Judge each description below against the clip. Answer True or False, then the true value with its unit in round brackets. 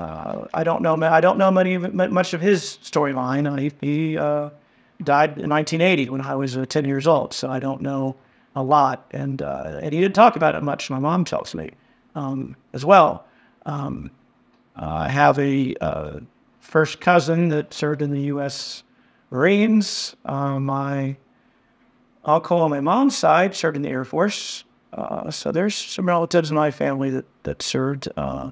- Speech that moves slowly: False (175 wpm)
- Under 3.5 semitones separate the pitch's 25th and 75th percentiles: False (4.1 semitones)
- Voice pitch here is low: False (150 Hz)